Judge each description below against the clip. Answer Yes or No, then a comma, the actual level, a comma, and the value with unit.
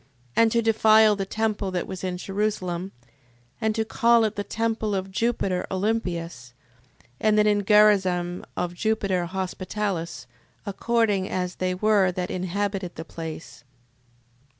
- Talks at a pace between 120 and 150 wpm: Yes, slow, 135 wpm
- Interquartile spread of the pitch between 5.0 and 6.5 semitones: No, average, 3.1 semitones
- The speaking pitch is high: Yes, high, 195 Hz